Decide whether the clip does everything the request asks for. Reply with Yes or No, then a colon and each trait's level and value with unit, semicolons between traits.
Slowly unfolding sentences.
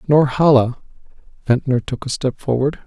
Yes: slow, 125 wpm